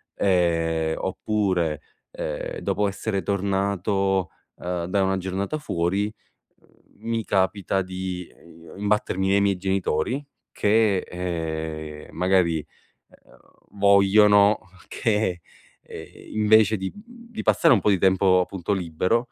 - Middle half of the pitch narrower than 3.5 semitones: Yes, average, 2.7 semitones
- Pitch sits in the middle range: No, very low, 95 Hz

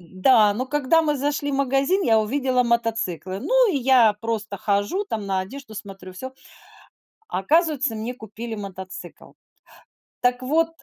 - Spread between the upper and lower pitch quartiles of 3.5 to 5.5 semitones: Yes, average, 5.2 semitones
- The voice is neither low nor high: No, high, 235 Hz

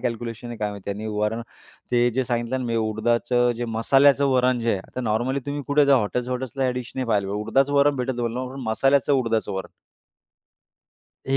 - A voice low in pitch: Yes, low, 120 Hz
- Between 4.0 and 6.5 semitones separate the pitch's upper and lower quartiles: No, average, 2.8 semitones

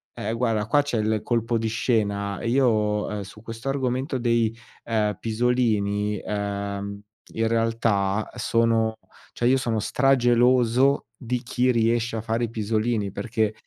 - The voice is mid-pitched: No, low, 115 Hz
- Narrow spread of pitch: Yes, narrow, 2.3 semitones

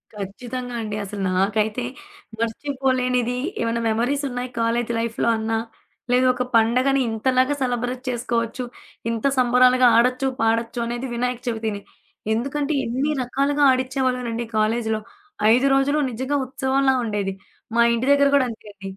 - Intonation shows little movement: Yes, narrow, 2.2 semitones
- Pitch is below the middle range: No, high, 245 Hz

